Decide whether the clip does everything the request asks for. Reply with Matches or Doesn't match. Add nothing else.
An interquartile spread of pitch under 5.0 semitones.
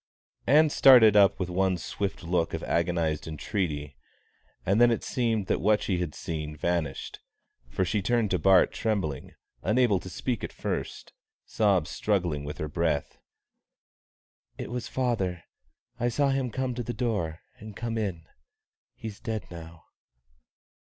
Doesn't match